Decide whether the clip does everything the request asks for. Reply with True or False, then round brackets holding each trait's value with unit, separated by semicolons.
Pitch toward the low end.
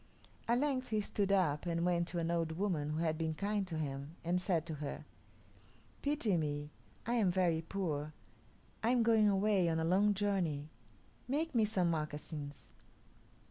False (175 Hz)